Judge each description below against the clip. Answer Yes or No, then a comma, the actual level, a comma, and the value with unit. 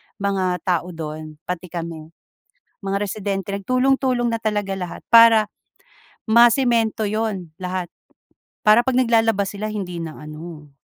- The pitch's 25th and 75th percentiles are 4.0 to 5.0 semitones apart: Yes, average, 4.4 semitones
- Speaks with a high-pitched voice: Yes, high, 200 Hz